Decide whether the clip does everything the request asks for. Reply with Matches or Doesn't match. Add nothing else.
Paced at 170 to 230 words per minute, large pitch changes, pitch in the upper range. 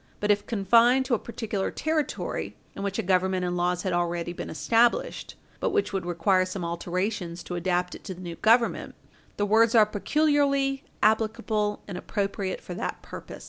Doesn't match